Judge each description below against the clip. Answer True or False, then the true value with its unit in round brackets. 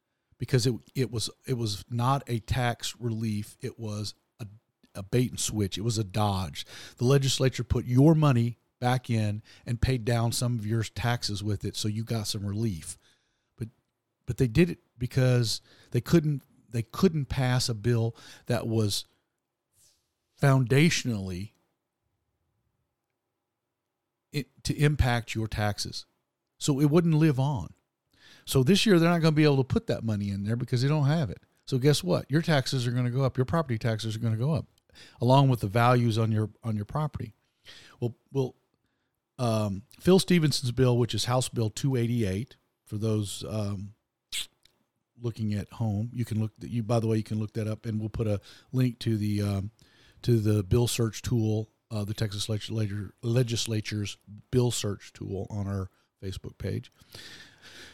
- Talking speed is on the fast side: False (175 wpm)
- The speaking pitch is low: True (115 Hz)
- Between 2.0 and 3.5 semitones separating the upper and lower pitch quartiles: True (3.0 semitones)